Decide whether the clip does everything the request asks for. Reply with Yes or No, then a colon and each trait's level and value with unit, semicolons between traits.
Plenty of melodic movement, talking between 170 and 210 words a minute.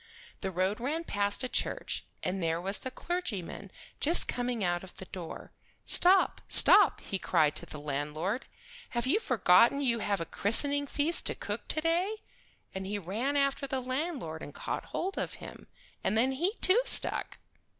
Yes: wide, 7.4 semitones; average, 175 wpm